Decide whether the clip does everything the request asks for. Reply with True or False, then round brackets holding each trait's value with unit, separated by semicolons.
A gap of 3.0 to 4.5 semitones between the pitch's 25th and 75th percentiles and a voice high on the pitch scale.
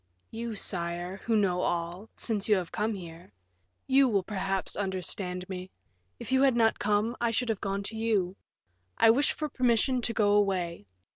True (3.8 semitones; 205 Hz)